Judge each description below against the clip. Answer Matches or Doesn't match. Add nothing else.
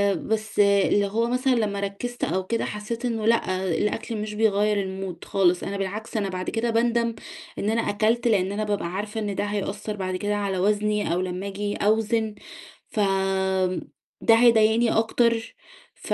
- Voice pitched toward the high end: Matches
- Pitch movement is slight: Matches